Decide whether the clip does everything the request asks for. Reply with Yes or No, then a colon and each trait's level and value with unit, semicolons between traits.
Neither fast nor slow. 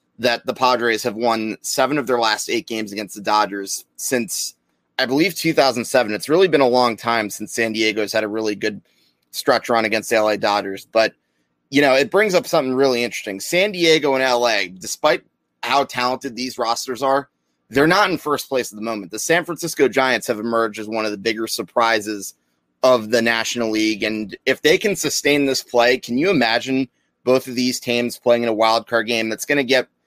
No: fast, 210 wpm